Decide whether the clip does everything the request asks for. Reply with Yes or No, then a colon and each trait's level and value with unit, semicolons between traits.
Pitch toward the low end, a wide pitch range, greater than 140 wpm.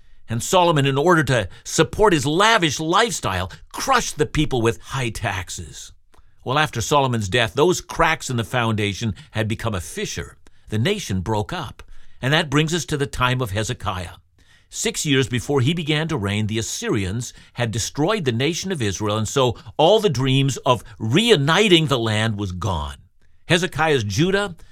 Yes: low, 125 Hz; wide, 6.6 semitones; average, 170 wpm